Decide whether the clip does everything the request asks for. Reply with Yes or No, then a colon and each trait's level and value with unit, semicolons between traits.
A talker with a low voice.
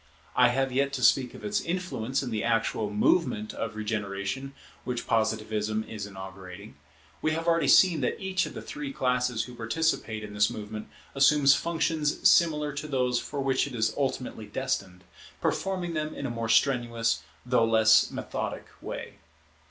Yes: low, 125 Hz